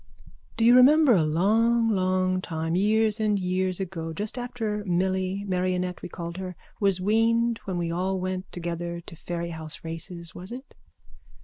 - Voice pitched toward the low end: No, medium, 185 Hz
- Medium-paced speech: Yes, average, 165 wpm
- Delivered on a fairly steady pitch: No, average, 3.7 semitones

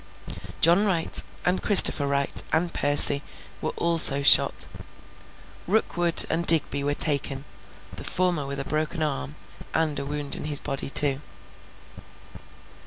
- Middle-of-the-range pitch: Yes, medium, 150 Hz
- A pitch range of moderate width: Yes, average, 3.2 semitones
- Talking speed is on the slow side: Yes, slow, 130 wpm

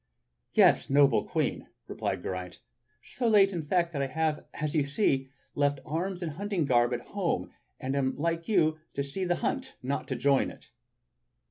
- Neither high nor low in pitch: Yes, medium, 150 Hz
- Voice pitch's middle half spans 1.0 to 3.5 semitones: No, average, 4.2 semitones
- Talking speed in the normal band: Yes, average, 180 wpm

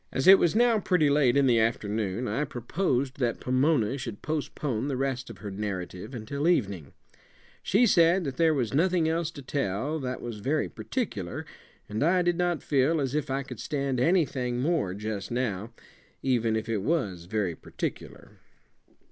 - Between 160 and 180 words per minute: Yes, average, 175 wpm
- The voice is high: No, low, 130 Hz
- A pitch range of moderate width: No, wide, 6.1 semitones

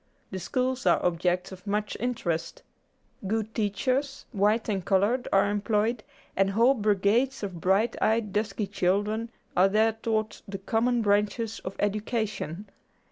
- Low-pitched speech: No, high, 210 Hz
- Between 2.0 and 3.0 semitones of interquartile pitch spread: Yes, narrow, 2.6 semitones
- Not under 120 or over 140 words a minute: Yes, slow, 135 wpm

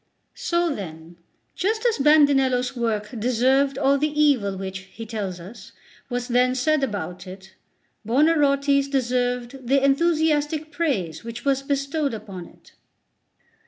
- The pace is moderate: No, slow, 125 wpm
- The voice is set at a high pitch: Yes, very high, 260 Hz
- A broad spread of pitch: No, average, 4.9 semitones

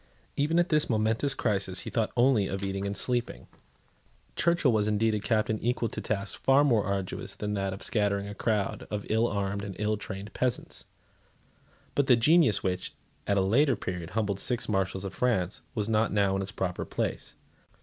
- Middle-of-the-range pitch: No, low, 105 Hz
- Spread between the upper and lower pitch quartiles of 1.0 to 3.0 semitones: No, average, 3.4 semitones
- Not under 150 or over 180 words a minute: No, average, 190 wpm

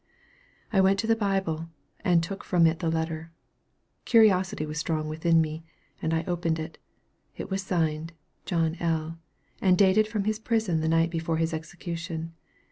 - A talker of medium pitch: Yes, medium, 165 Hz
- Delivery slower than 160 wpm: No, average, 165 wpm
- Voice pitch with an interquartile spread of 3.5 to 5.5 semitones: No, average, 2.9 semitones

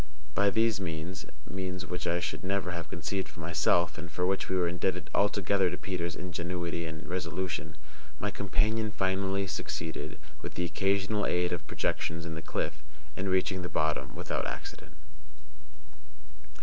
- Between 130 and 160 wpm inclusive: Yes, average, 155 wpm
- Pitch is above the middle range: No, very low, 90 Hz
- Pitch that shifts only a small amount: Yes, narrow, 2.2 semitones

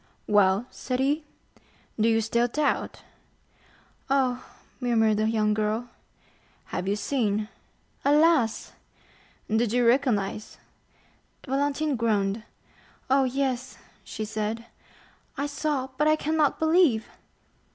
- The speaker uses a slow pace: Yes, slow, 105 wpm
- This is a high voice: Yes, high, 245 Hz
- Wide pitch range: No, average, 4.4 semitones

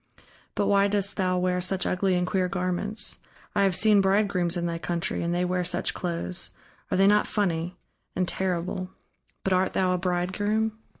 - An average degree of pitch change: No, narrow, 1.9 semitones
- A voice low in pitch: No, medium, 185 Hz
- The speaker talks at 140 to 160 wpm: No, average, 180 wpm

